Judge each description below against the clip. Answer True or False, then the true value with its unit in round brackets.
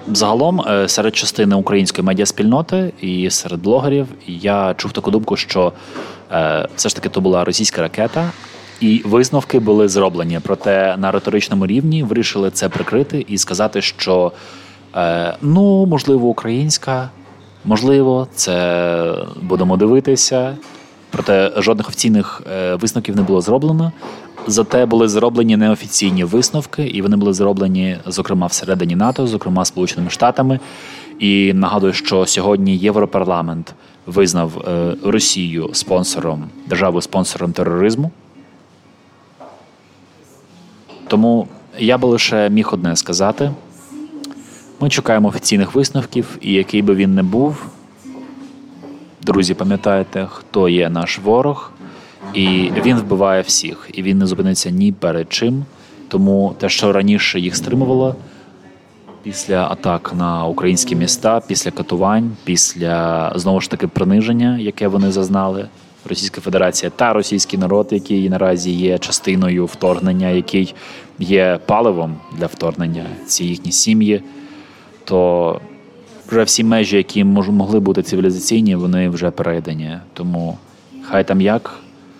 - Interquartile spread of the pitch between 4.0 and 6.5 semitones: True (4.6 semitones)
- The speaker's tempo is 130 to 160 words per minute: False (120 wpm)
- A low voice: True (100 Hz)